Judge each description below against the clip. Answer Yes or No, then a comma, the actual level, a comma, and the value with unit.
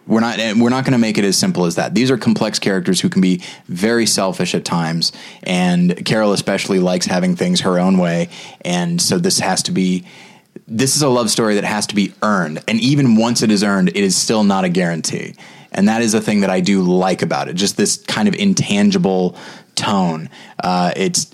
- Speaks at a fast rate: Yes, fast, 220 wpm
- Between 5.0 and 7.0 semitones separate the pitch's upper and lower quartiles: Yes, wide, 5.6 semitones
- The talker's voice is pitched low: Yes, low, 105 Hz